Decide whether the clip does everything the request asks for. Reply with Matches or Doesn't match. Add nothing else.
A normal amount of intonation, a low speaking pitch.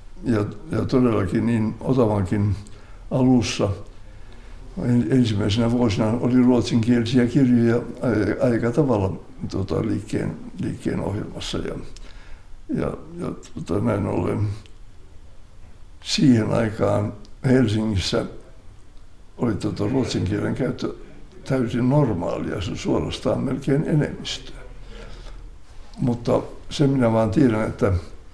Matches